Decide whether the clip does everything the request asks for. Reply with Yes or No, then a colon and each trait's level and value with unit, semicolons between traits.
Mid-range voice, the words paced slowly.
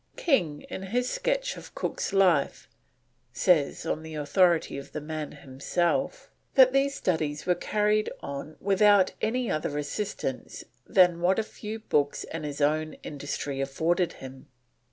No: medium, 170 Hz; average, 145 wpm